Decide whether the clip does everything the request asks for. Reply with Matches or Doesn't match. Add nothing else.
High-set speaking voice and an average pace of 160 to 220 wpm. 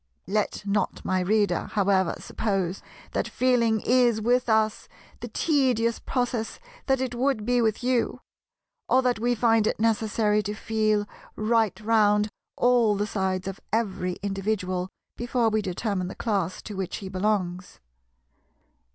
Doesn't match